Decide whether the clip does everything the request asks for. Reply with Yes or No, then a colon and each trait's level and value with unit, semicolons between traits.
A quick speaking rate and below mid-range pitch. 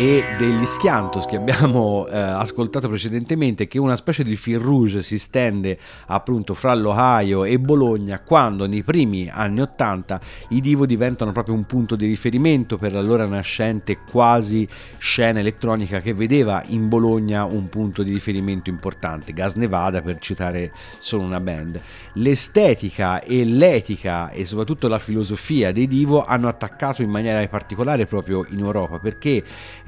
No: average, 150 wpm; low, 110 Hz